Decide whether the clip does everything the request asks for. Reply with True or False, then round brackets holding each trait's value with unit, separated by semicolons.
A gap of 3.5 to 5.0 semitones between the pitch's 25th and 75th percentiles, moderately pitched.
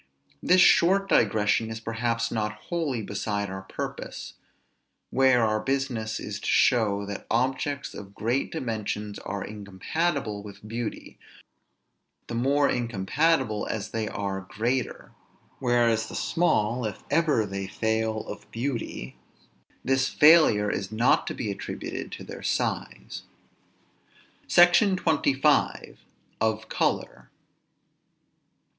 False (4.3 semitones; 115 Hz)